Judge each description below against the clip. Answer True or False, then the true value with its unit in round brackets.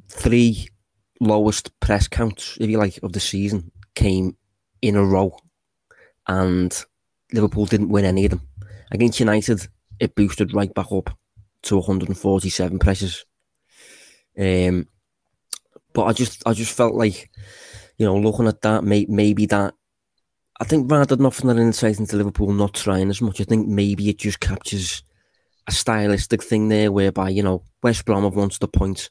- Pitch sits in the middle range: False (105 Hz)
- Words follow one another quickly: False (165 wpm)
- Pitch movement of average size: False (2.2 semitones)